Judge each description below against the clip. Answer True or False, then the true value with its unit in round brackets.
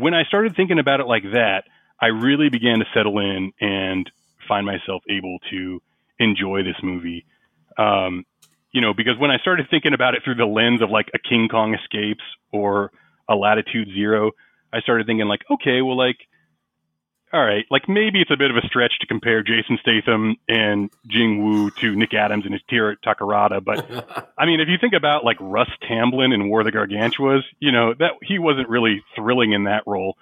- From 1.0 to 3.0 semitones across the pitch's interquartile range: False (3.7 semitones)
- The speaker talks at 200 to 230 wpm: True (205 wpm)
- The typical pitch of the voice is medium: False (110 Hz)